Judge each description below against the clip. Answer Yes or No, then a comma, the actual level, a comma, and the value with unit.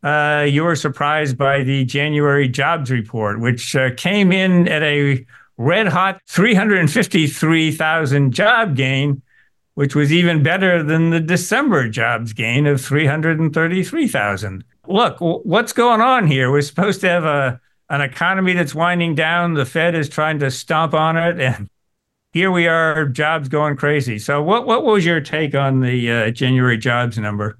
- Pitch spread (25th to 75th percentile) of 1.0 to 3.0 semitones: No, average, 4.1 semitones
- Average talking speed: Yes, average, 160 wpm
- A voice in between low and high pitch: Yes, medium, 150 Hz